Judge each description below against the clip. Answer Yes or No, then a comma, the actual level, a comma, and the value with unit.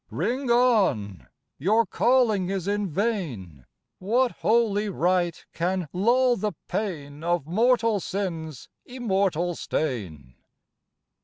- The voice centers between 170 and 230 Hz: Yes, high, 190 Hz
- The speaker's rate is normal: No, slow, 100 wpm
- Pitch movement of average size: No, wide, 6.0 semitones